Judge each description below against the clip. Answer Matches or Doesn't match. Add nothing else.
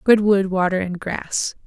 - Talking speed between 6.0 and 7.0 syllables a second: Doesn't match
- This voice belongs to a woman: Matches